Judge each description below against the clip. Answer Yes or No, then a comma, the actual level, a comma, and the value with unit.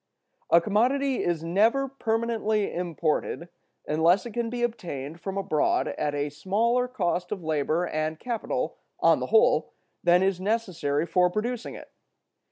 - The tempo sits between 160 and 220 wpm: No, average, 145 wpm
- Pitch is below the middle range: No, high, 190 Hz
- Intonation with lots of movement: Yes, wide, 5.7 semitones